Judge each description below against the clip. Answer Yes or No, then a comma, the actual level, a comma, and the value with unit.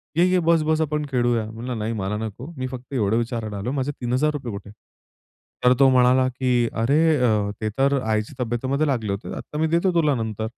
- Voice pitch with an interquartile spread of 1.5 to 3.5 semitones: No, average, 4.1 semitones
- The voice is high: No, low, 125 Hz